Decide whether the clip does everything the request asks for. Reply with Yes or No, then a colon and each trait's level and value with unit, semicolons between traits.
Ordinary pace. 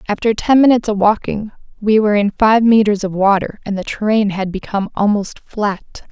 Yes: average, 185 wpm